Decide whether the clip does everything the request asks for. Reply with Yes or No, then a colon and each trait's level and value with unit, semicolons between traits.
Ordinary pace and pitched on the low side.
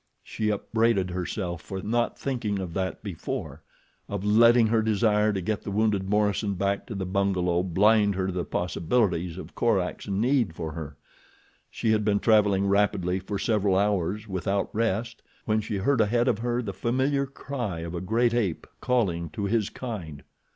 Yes: average, 170 wpm; low, 100 Hz